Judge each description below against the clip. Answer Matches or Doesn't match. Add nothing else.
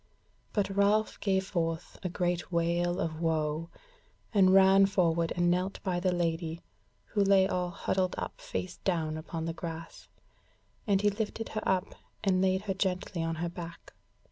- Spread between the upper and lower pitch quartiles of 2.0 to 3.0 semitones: Matches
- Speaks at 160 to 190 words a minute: Matches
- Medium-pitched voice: Matches